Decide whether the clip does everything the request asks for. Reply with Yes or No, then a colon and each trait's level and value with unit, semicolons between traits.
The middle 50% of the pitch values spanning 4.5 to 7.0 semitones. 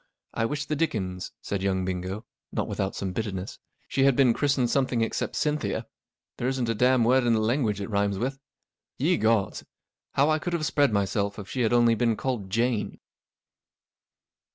Yes: average, 4.8 semitones